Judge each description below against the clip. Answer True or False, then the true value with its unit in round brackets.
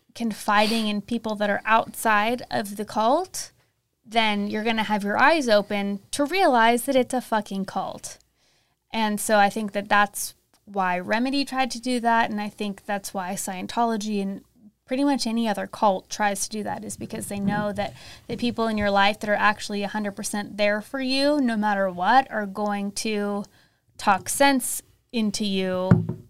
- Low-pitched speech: False (215 Hz)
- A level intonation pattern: True (2.3 semitones)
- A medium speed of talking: True (180 wpm)